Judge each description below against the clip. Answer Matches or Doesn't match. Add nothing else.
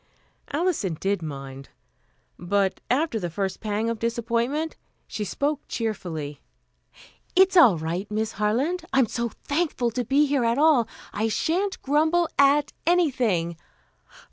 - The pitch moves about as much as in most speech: Doesn't match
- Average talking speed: Doesn't match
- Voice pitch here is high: Matches